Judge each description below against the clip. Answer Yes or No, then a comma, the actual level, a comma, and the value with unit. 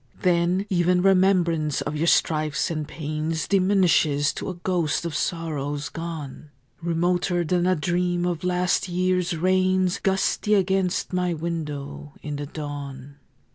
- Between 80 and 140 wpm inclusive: Yes, slow, 135 wpm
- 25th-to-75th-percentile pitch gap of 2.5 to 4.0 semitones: Yes, average, 3.1 semitones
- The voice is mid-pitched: Yes, medium, 170 Hz